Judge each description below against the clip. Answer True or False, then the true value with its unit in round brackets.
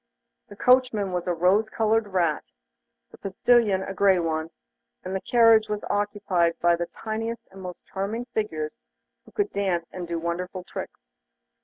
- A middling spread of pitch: True (3.8 semitones)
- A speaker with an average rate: True (160 wpm)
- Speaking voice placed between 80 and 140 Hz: False (195 Hz)